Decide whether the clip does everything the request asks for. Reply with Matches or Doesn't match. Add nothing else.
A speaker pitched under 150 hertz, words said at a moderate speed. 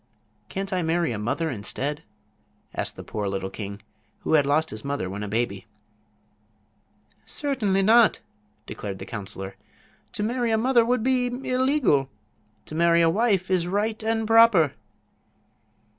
Doesn't match